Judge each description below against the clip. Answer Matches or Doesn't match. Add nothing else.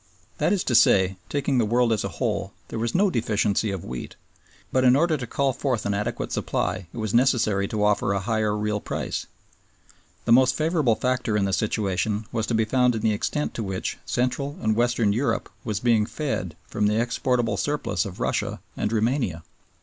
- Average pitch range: Matches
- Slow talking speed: Doesn't match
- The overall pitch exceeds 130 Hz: Doesn't match